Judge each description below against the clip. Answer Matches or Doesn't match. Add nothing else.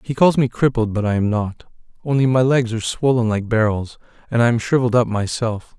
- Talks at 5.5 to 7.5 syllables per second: Matches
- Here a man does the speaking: Matches